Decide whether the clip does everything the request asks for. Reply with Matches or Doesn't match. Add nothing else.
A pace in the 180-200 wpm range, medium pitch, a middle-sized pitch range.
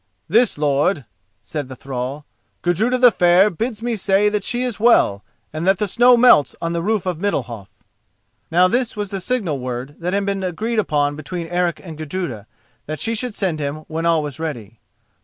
Doesn't match